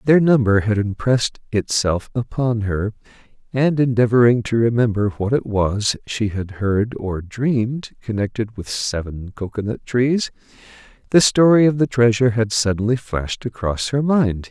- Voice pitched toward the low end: Yes, low, 115 Hz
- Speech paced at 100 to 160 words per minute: Yes, average, 150 wpm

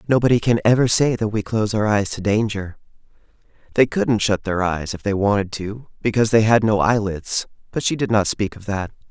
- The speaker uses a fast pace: Yes, fast, 210 wpm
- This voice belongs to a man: Yes, male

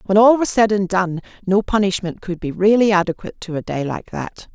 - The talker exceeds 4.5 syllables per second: Yes, 5.6 syllables/s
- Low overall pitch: No, high, 195 Hz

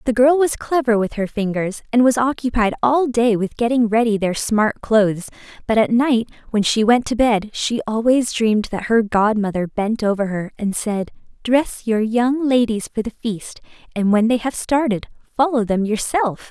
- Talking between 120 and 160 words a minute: No, average, 190 wpm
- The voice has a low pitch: No, high, 225 Hz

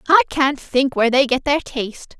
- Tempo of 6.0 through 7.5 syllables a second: No, 5.3 syllables/s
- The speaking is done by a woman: Yes, female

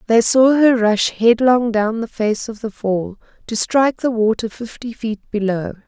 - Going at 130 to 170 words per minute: No, average, 185 wpm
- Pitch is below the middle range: No, high, 225 Hz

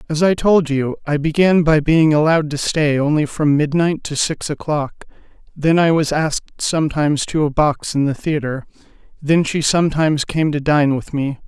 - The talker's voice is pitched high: No, medium, 150 Hz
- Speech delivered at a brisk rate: No, average, 190 wpm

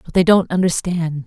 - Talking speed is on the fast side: No, average, 190 wpm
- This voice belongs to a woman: Yes, female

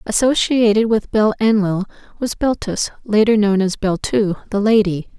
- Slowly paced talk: Yes, slow, 125 wpm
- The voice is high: Yes, high, 210 Hz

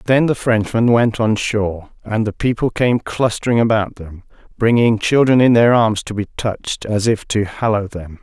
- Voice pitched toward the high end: No, low, 110 Hz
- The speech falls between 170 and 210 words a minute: Yes, average, 190 wpm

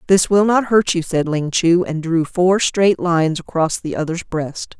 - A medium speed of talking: No, fast, 215 wpm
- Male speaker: No, female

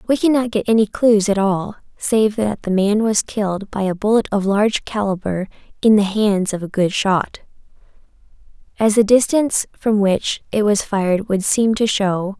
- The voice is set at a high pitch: Yes, high, 205 Hz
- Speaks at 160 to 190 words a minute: Yes, average, 185 wpm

